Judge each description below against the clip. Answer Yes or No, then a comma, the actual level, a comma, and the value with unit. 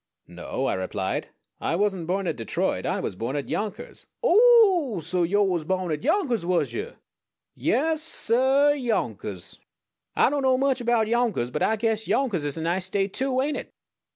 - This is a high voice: Yes, high, 210 Hz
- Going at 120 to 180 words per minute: No, average, 190 wpm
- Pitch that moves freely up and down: Yes, wide, 8.1 semitones